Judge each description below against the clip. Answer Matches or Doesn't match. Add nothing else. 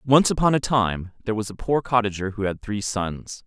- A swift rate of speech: Matches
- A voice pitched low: Matches